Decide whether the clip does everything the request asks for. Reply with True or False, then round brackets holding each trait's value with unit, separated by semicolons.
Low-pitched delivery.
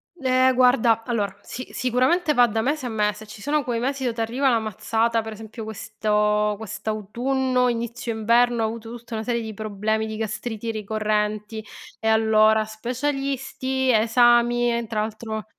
False (225 Hz)